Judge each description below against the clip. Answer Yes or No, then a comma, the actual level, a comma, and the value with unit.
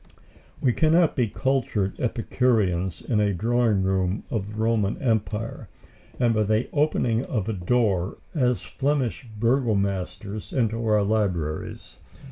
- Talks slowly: Yes, slow, 130 wpm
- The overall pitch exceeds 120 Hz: No, low, 110 Hz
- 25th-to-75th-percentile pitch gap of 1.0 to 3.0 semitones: No, average, 3.8 semitones